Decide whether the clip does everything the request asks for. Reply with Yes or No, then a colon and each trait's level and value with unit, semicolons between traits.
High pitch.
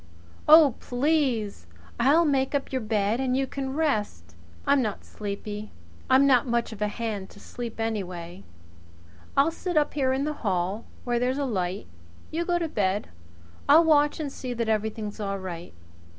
Yes: high, 235 Hz